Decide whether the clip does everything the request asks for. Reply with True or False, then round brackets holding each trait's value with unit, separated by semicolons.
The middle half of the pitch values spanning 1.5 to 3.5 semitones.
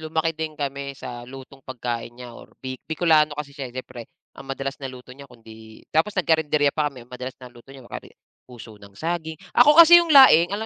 False (4.2 semitones)